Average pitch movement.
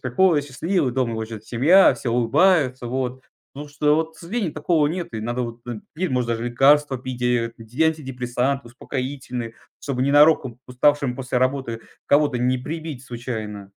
Yes: average, 3.4 semitones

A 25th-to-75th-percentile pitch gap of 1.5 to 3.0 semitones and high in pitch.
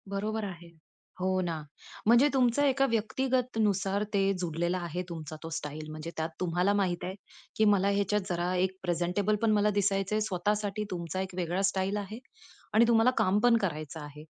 No: average, 3.5 semitones; high, 195 Hz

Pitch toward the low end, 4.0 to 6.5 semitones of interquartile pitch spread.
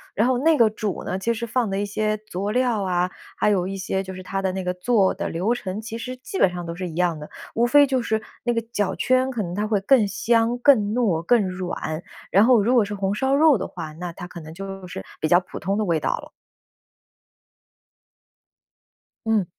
No: high, 205 Hz; average, 4.4 semitones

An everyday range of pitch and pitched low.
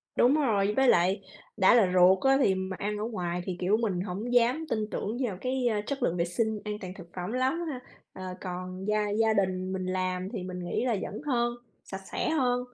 No: average, 4.6 semitones; high, 205 Hz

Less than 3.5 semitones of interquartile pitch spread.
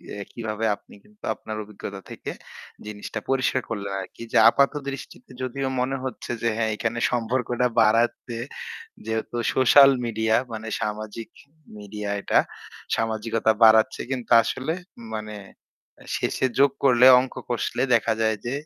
Yes: average, 2.8 semitones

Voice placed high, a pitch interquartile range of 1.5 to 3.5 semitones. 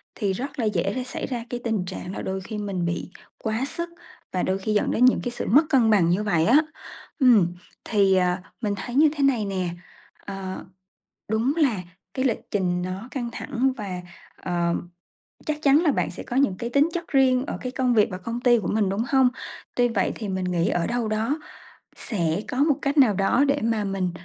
No: high, 220 Hz; average, 5.3 semitones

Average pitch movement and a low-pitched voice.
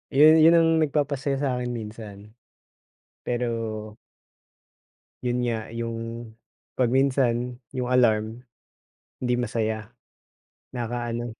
No: narrow, 2.2 semitones; low, 120 Hz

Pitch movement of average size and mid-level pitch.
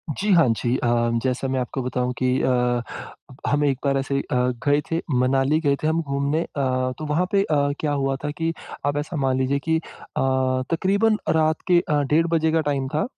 Yes: average, 3.3 semitones; medium, 145 Hz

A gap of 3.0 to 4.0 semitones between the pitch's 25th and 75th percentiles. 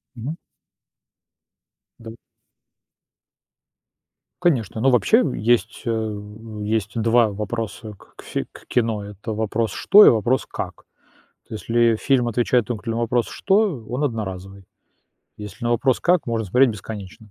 No: narrow, 2.4 semitones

